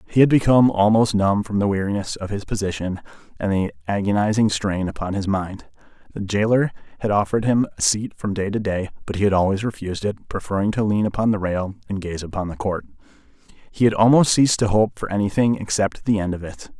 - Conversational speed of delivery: No, fast, 210 wpm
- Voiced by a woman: No, male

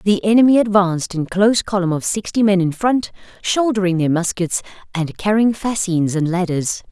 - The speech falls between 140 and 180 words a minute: Yes, average, 165 wpm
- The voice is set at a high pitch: Yes, high, 195 Hz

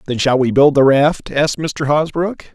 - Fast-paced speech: Yes, fast, 215 wpm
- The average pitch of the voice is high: No, medium, 145 Hz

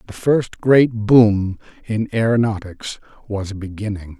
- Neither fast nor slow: No, slow, 115 wpm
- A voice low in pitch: Yes, low, 105 Hz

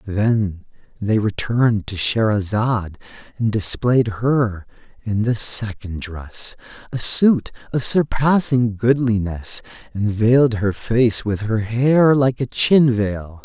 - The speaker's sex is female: No, male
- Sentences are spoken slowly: Yes, slow, 125 wpm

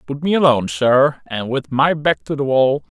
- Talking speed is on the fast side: Yes, fast, 220 wpm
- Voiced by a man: Yes, male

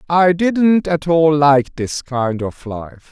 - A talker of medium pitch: Yes, medium, 150 Hz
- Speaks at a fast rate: No, average, 195 wpm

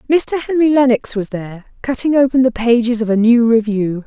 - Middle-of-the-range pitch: No, high, 240 Hz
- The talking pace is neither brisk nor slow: Yes, average, 190 wpm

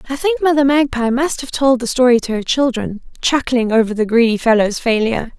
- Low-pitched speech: No, very high, 250 Hz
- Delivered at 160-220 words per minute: Yes, average, 200 wpm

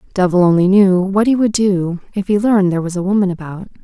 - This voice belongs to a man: No, female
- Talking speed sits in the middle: No, fast, 235 wpm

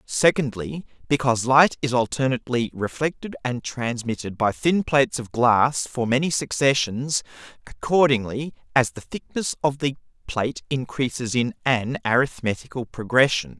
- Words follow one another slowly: Yes, slow, 125 wpm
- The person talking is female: No, male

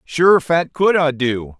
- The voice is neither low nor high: Yes, medium, 150 Hz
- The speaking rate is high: No, average, 190 wpm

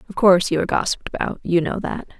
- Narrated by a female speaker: Yes, female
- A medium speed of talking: No, fast, 220 wpm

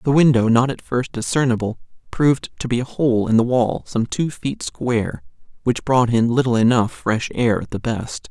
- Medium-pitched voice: No, low, 120 Hz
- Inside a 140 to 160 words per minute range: No, average, 200 wpm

